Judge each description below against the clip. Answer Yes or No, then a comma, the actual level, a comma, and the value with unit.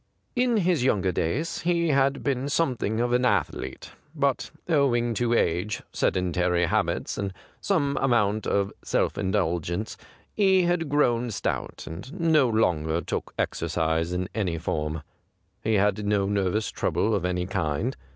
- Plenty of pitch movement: Yes, wide, 7.5 semitones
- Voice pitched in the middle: No, low, 110 Hz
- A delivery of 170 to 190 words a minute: No, average, 140 wpm